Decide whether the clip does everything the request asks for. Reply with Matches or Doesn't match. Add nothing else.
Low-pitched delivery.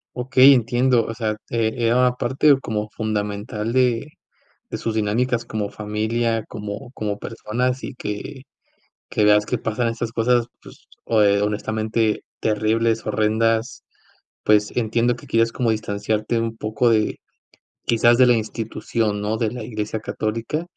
Matches